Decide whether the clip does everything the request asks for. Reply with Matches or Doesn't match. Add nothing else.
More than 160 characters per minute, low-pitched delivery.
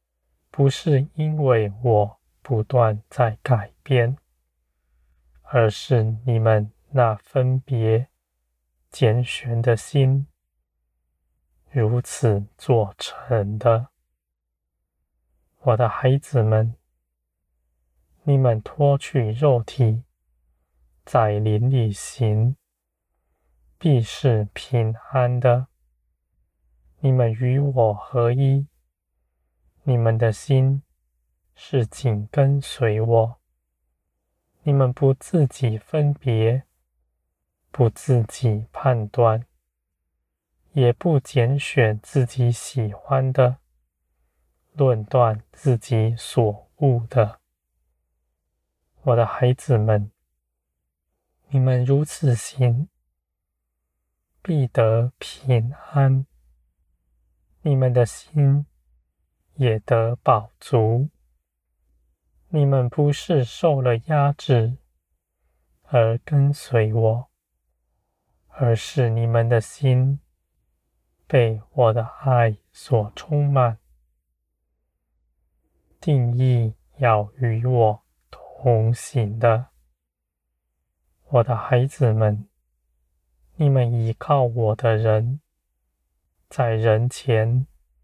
Doesn't match